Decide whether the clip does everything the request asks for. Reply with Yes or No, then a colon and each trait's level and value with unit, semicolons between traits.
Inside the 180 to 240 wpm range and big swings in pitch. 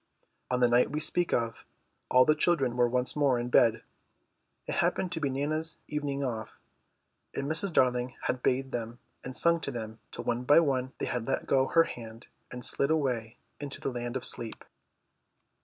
No: average, 190 wpm; average, 3.2 semitones